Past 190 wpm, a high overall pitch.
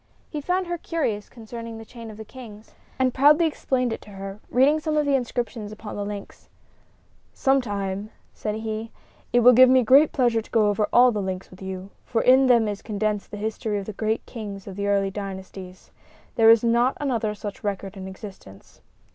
Yes: average, 200 wpm; high, 220 Hz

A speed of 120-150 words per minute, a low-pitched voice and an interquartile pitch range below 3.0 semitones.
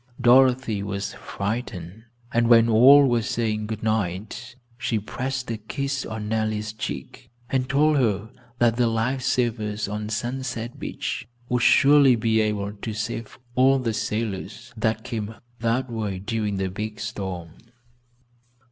Yes: average, 140 wpm; low, 110 Hz; narrow, 2.6 semitones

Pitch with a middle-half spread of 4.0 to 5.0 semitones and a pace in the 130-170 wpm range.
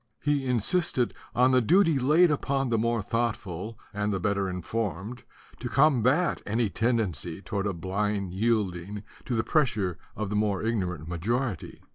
Yes: average, 4.4 semitones; average, 155 wpm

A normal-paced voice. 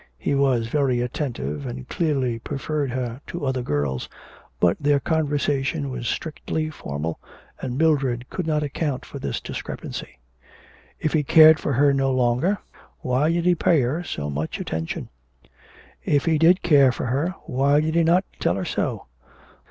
Yes: average, 160 wpm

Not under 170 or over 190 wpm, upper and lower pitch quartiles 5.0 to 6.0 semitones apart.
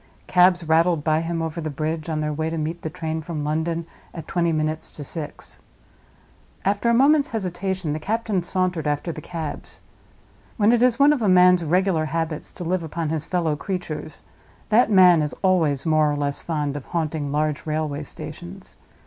No: average, 185 wpm; average, 2.9 semitones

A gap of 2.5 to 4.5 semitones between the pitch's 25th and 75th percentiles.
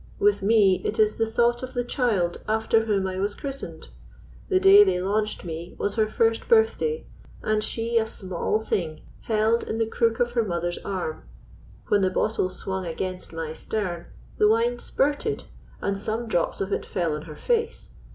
Yes: average, 4.1 semitones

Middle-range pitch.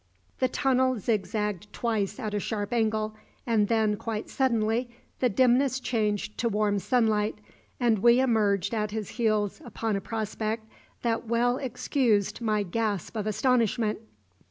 No: high, 220 Hz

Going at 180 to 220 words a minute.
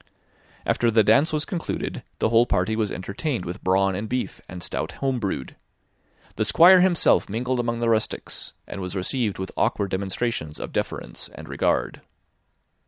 No: average, 165 wpm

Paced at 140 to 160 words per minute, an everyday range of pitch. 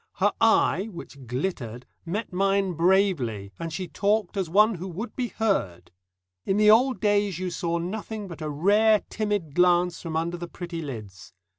No: average, 170 wpm; average, 4.1 semitones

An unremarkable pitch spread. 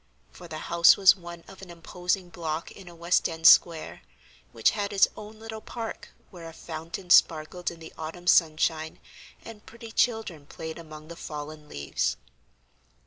Yes: average, 3.2 semitones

